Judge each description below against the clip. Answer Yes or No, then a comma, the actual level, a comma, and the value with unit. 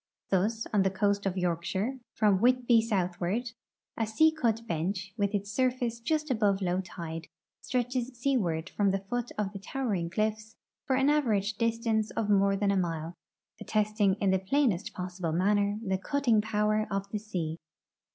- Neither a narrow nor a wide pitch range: Yes, average, 3.4 semitones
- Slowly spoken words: No, average, 165 wpm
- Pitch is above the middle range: Yes, high, 210 Hz